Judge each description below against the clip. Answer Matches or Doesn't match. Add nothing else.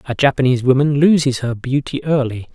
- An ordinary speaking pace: Matches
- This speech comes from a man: Matches